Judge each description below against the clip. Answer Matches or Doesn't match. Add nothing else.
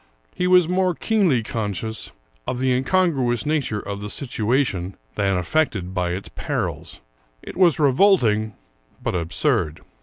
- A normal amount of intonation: Doesn't match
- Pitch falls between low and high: Doesn't match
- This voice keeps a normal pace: Doesn't match